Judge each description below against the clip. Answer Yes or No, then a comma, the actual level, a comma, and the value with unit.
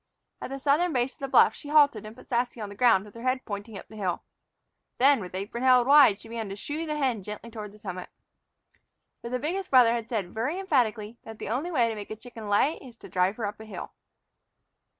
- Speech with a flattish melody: No, average, 4.1 semitones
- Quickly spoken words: Yes, fast, 245 wpm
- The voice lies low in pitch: No, high, 235 Hz